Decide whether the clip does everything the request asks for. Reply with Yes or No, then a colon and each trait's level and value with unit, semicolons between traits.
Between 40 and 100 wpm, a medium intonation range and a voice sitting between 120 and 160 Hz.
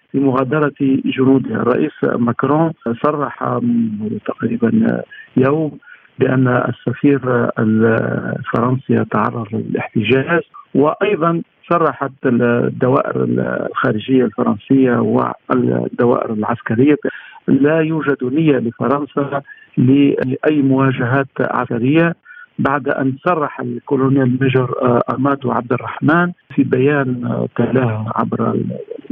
Yes: average, 80 wpm; average, 3.4 semitones; low, 135 Hz